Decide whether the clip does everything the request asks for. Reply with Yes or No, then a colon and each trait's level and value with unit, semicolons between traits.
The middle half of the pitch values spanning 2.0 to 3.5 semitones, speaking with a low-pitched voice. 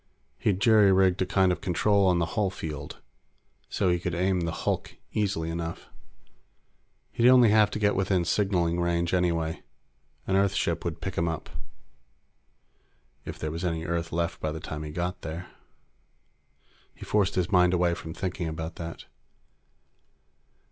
Yes: narrow, 2.6 semitones; very low, 90 Hz